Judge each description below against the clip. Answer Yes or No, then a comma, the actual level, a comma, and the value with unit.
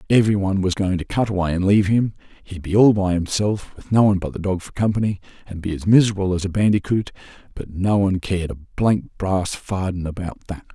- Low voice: Yes, very low, 95 Hz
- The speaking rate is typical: No, fast, 225 wpm